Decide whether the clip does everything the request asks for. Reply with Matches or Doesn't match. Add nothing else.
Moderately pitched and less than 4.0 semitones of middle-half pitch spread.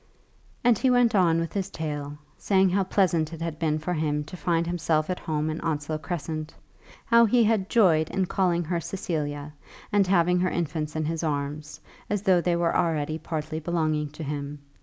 Matches